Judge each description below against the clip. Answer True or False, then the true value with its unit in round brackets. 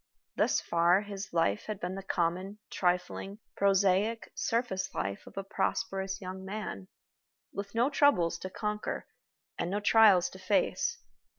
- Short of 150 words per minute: True (140 wpm)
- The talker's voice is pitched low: False (195 Hz)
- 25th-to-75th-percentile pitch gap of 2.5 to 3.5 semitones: True (2.8 semitones)